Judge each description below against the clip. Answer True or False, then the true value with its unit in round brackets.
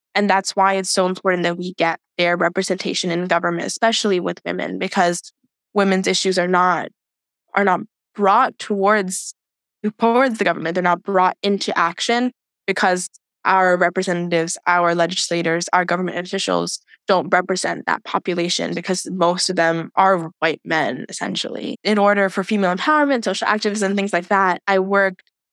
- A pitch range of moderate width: False (2.2 semitones)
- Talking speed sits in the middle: True (155 wpm)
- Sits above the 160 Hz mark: True (185 Hz)